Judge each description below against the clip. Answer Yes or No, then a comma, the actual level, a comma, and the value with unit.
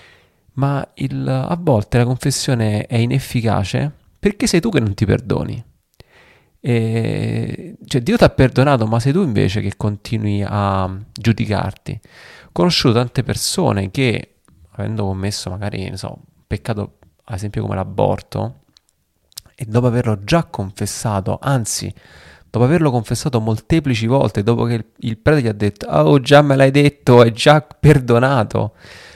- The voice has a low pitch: Yes, low, 115 Hz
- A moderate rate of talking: Yes, average, 145 wpm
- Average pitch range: Yes, average, 4.6 semitones